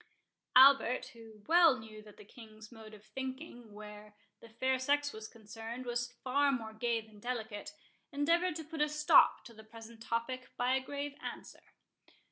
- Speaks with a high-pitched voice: Yes, high, 240 Hz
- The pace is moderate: Yes, average, 170 wpm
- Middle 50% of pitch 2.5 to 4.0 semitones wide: Yes, average, 3.7 semitones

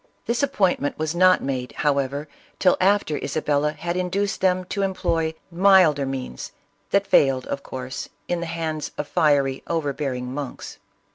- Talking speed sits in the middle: Yes, average, 145 wpm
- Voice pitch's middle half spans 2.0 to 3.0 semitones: No, average, 4.7 semitones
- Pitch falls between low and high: Yes, medium, 155 Hz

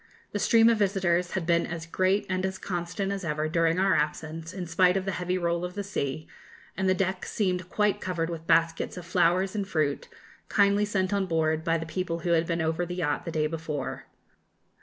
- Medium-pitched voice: Yes, medium, 175 Hz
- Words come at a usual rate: No, fast, 215 wpm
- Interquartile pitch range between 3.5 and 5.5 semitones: No, narrow, 2.5 semitones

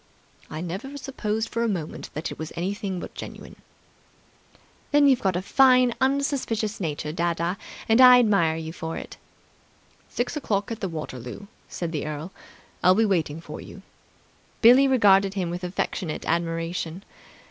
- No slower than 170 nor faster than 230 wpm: No, average, 155 wpm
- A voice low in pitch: No, high, 190 Hz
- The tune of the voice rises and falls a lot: Yes, wide, 5.8 semitones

